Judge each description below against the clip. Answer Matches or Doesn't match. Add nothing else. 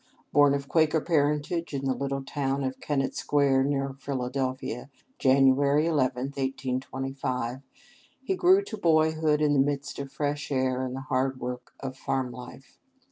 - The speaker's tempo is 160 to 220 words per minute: Doesn't match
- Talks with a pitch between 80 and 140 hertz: Matches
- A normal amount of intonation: Doesn't match